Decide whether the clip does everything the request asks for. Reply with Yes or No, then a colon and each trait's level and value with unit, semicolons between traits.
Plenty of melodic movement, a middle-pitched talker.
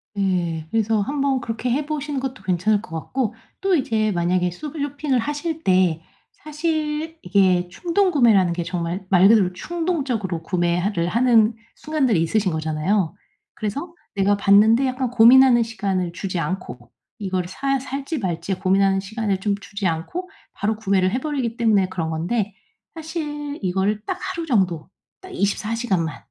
No: wide, 6.7 semitones; high, 210 Hz